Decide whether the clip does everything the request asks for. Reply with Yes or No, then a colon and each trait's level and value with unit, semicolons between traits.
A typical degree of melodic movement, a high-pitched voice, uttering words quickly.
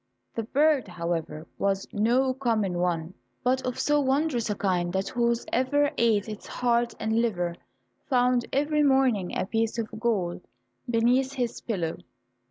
No: average, 4.9 semitones; high, 230 Hz; average, 145 wpm